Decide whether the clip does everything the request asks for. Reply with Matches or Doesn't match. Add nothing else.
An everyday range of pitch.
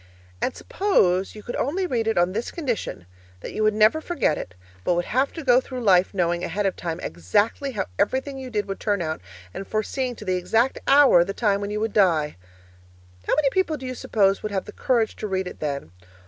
Doesn't match